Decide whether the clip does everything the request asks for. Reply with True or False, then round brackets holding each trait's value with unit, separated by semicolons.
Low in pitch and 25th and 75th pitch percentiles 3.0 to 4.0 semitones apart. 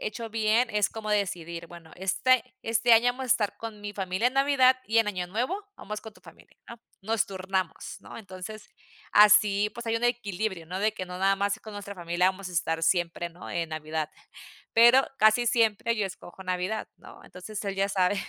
False (205 Hz; 3.6 semitones)